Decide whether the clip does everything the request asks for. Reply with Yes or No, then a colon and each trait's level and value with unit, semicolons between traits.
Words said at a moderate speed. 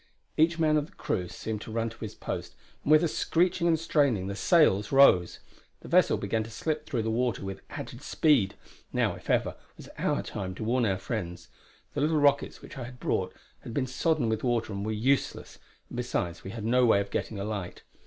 No: fast, 220 wpm